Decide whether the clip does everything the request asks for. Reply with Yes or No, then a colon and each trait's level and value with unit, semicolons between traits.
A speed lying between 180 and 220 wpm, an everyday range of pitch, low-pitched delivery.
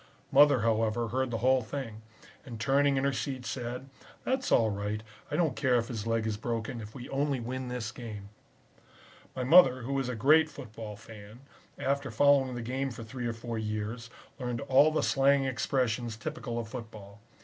Yes: average, 185 wpm; average, 3.3 semitones; low, 125 Hz